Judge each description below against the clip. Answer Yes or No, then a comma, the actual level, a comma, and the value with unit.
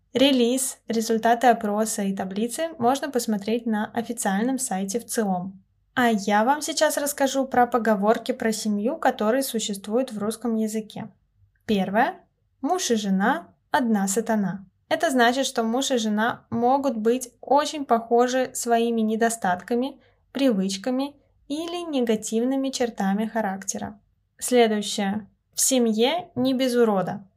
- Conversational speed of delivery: Yes, average, 120 wpm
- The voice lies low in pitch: No, high, 235 Hz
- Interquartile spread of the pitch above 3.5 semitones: No, average, 3.2 semitones